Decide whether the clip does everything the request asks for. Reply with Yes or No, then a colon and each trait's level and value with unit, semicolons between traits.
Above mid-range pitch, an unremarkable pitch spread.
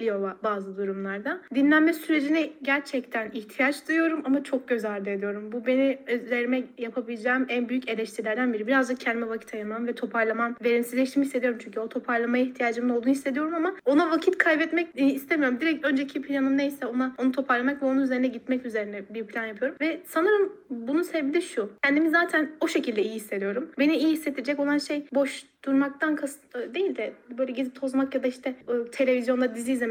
Yes: very high, 260 Hz; average, 3.5 semitones